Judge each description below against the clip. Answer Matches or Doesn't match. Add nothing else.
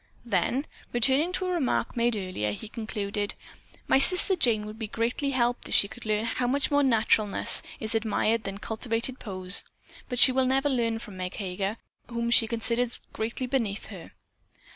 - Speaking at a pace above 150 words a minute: Matches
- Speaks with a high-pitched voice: Matches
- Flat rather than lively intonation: Doesn't match